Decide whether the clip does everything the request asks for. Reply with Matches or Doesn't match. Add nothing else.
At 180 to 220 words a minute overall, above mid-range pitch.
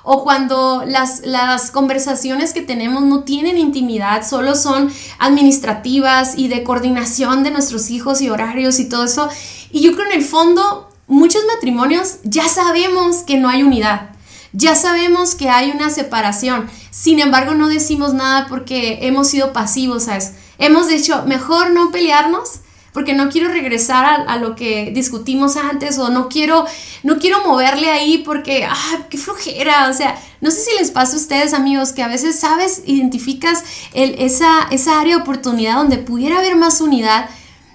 Doesn't match